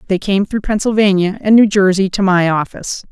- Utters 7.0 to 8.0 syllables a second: No, 5.6 syllables/s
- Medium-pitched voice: No, high, 195 Hz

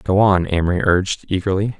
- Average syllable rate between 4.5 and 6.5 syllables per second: Yes, 5.7 syllables/s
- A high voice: No, very low, 95 Hz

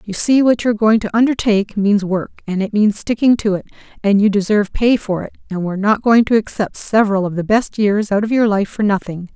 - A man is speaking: No, female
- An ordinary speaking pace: No, fast, 250 wpm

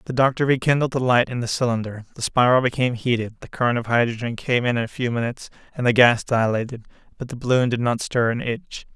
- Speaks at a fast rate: Yes, fast, 220 wpm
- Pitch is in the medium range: No, low, 120 Hz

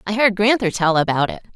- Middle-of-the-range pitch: No, high, 200 Hz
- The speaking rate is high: Yes, fast, 230 wpm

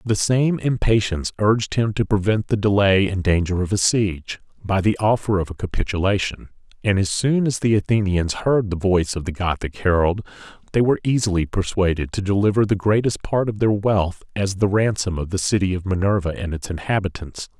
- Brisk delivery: No, average, 190 wpm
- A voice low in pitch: Yes, low, 100 Hz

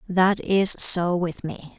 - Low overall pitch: No, medium, 180 Hz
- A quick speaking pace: No, average, 170 wpm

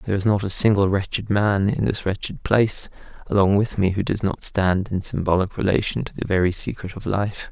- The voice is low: Yes, low, 100 Hz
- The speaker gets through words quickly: Yes, fast, 215 wpm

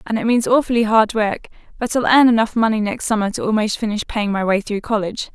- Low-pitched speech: No, high, 220 Hz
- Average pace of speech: No, fast, 235 wpm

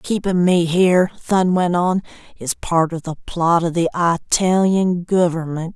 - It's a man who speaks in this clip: No, female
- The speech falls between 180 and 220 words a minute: No, average, 155 wpm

